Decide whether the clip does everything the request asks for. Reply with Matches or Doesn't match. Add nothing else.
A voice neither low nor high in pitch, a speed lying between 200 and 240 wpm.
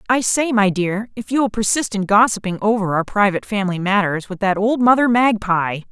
Doesn't match